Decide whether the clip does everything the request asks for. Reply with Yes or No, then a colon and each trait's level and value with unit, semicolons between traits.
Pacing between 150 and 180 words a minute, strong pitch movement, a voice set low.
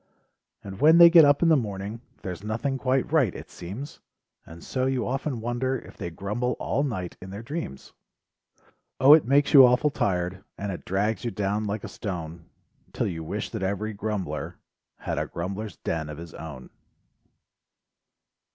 Yes: average, 175 wpm; wide, 5.8 semitones; low, 105 Hz